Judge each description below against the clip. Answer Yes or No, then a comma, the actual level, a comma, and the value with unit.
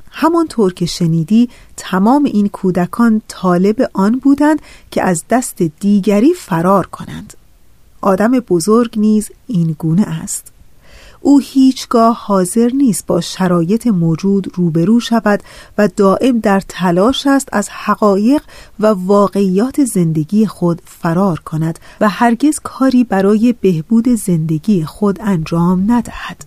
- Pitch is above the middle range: Yes, high, 205 Hz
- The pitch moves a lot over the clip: No, average, 4.5 semitones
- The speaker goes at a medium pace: Yes, average, 120 wpm